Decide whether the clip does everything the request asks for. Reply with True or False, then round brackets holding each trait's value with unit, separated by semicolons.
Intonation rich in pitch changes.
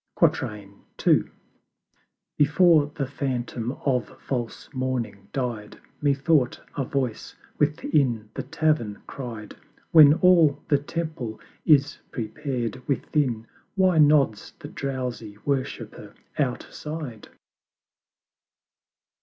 False (4.1 semitones)